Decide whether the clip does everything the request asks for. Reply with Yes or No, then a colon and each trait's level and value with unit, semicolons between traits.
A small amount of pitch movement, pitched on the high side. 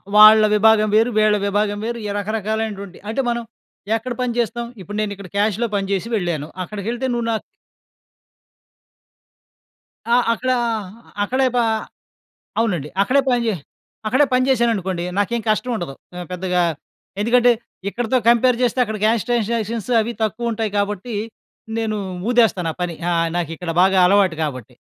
No: average, 3.4 semitones; high, 215 Hz